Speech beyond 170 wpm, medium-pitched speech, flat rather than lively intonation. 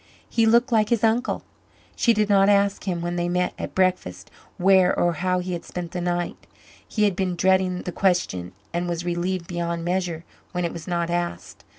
Yes: average, 200 wpm; medium, 180 Hz; narrow, 2.0 semitones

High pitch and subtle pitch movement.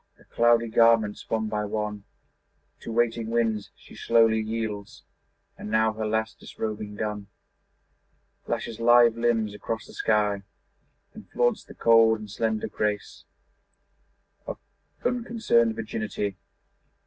No: low, 110 Hz; narrow, 1.5 semitones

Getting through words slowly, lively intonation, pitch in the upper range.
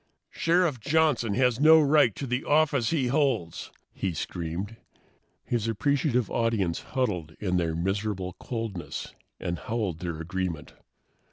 No: slow, 125 wpm; wide, 7.0 semitones; low, 115 Hz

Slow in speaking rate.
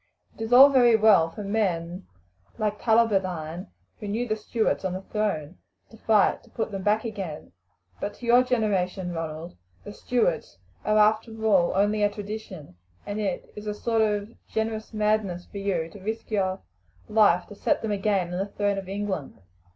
No: average, 180 wpm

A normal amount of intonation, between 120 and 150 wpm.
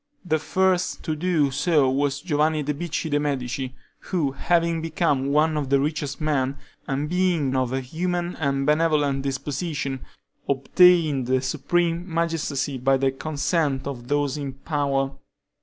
Yes: average, 3.3 semitones; average, 145 wpm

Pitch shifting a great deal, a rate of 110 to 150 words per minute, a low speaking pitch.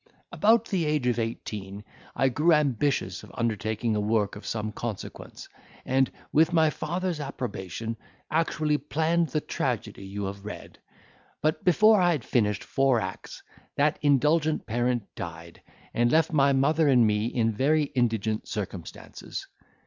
Yes: wide, 6.1 semitones; average, 145 wpm; low, 130 Hz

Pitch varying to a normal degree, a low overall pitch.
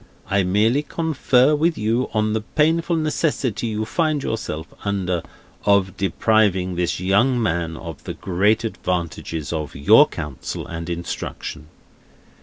No: wide, 6.5 semitones; low, 105 Hz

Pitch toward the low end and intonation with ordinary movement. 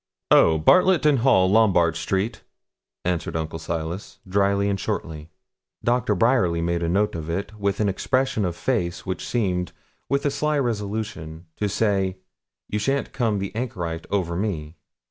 Yes: low, 100 Hz; average, 4.6 semitones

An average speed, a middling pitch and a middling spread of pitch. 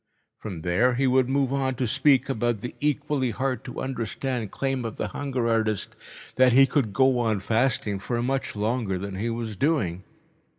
No: average, 180 wpm; low, 120 Hz; average, 3.6 semitones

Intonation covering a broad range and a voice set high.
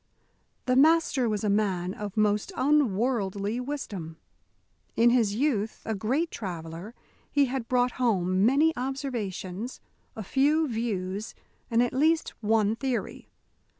No: average, 4.9 semitones; high, 230 Hz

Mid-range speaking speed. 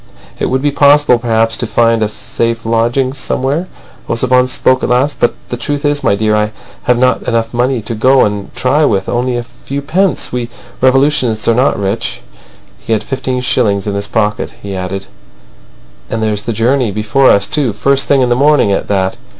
Yes: average, 190 wpm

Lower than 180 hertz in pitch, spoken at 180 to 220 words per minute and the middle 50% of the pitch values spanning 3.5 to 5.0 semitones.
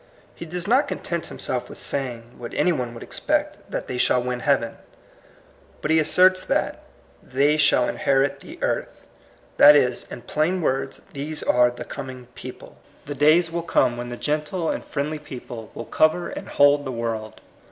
Yes: medium, 140 Hz; average, 185 wpm; average, 4.1 semitones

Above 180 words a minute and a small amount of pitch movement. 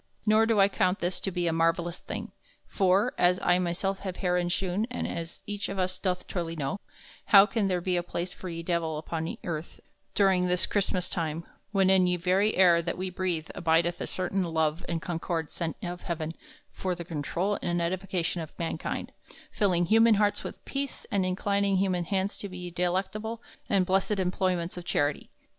Yes: average, 190 wpm; narrow, 2.2 semitones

